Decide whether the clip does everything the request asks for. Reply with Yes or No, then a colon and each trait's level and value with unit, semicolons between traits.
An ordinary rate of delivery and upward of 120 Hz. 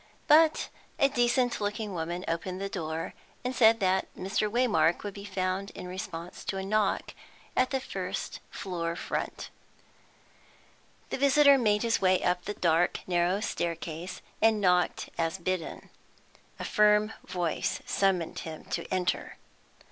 Yes: average, 145 wpm; high, 190 Hz